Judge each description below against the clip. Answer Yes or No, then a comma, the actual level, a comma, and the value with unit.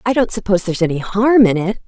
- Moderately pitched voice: No, high, 205 Hz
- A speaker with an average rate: No, fast, 255 wpm